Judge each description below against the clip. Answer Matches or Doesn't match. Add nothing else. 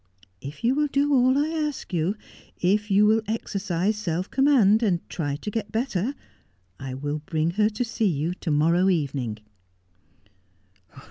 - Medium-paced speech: Matches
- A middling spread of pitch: Doesn't match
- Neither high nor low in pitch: Doesn't match